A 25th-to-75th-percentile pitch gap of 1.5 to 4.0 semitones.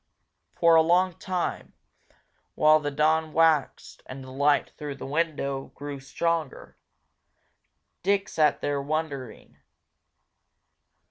Yes: average, 2.7 semitones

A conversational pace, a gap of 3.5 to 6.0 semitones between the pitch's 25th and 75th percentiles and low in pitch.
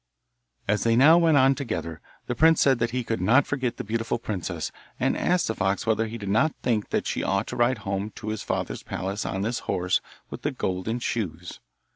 No: fast, 215 wpm; average, 4.4 semitones; low, 115 Hz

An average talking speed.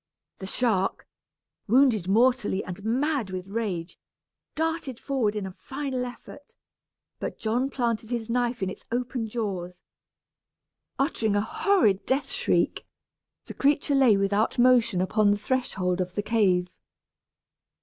No: slow, 130 wpm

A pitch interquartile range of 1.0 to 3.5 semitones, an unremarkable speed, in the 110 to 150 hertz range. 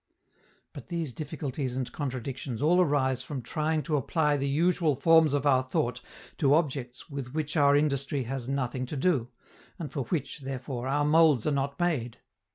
Yes: average, 2.9 semitones; average, 170 wpm; medium, 140 Hz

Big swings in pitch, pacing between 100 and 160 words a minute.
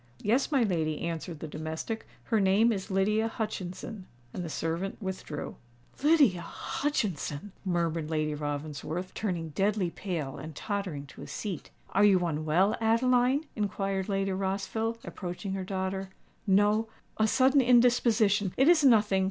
No: average, 4.6 semitones; slow, 135 wpm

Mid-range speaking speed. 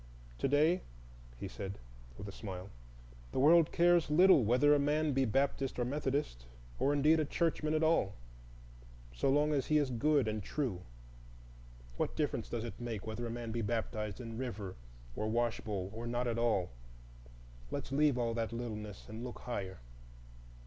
Yes: average, 170 wpm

